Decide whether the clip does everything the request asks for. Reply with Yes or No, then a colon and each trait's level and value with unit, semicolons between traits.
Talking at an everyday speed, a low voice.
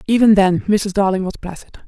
No: average, 190 wpm; high, 200 Hz